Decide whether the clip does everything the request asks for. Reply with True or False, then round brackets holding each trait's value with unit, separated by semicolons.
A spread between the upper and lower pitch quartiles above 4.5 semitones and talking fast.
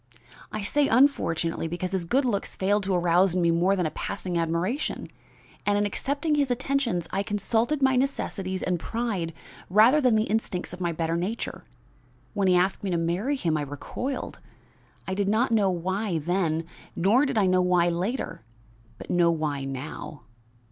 False (5.1 semitones; 175 wpm)